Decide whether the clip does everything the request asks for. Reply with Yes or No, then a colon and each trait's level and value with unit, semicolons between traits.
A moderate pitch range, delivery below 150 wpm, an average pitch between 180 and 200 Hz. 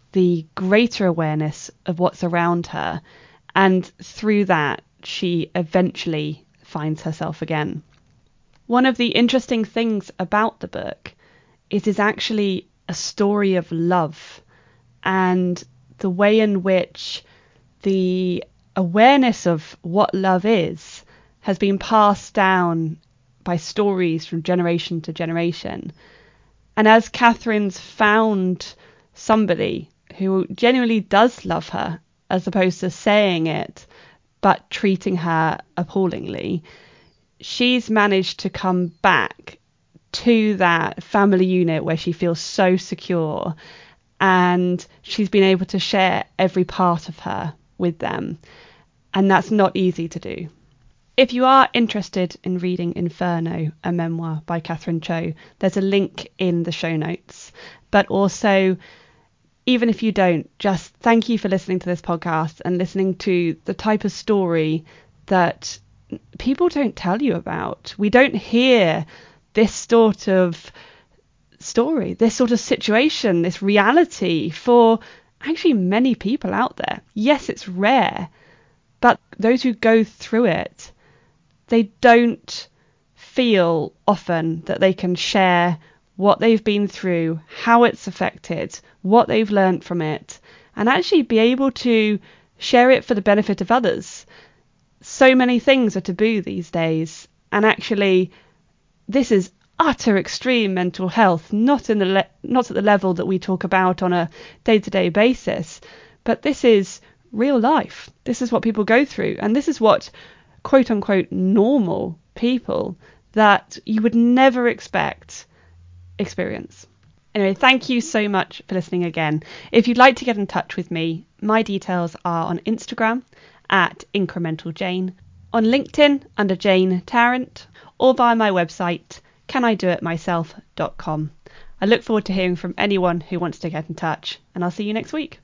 Yes: average, 4.3 semitones; average, 140 wpm; high, 190 Hz